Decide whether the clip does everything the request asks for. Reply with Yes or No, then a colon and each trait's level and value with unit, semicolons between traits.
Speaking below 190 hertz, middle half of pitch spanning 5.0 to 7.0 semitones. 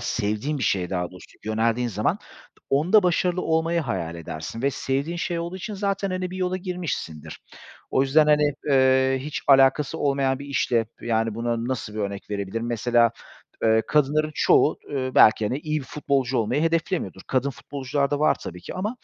Yes: low, 135 Hz; wide, 5.6 semitones